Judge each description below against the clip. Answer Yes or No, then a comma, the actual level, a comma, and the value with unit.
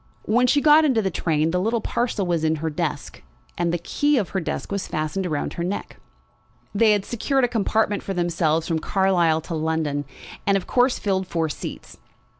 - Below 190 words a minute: No, average, 200 wpm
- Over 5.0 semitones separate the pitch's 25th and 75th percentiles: Yes, wide, 5.4 semitones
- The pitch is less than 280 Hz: Yes, high, 190 Hz